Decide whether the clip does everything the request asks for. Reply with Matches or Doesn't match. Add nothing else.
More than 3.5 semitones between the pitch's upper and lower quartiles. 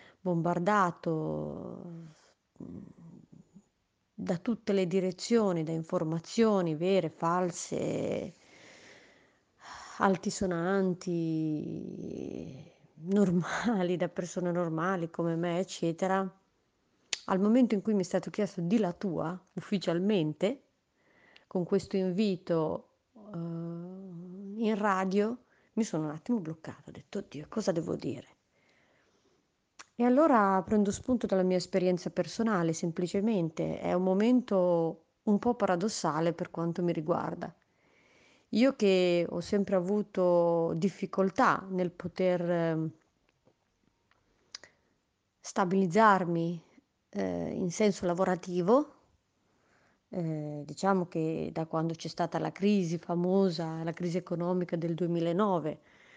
Doesn't match